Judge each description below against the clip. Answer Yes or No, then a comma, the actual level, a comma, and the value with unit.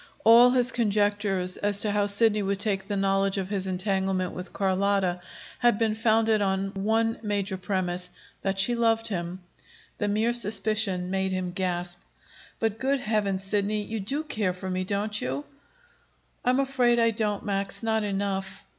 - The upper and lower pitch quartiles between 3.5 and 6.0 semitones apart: No, narrow, 2.6 semitones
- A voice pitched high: Yes, high, 200 Hz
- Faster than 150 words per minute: Yes, average, 165 wpm